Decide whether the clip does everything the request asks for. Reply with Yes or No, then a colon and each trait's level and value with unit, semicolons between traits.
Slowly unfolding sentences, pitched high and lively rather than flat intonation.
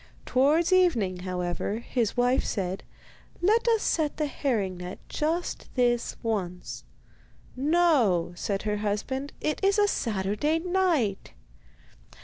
Yes: slow, 120 wpm; high, 245 Hz; wide, 8.6 semitones